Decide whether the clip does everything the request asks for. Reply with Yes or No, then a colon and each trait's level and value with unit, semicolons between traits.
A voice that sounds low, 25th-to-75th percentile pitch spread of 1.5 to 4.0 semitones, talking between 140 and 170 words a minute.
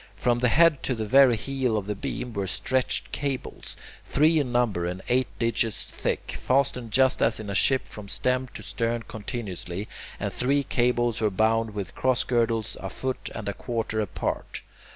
No: low, 120 Hz; average, 3.2 semitones; average, 180 wpm